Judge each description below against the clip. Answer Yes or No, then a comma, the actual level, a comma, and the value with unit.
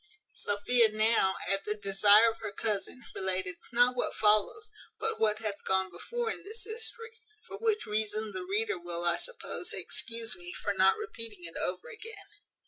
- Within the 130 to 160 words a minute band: No, average, 170 wpm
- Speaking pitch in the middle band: No, high, 215 Hz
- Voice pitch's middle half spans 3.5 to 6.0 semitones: Yes, average, 4.6 semitones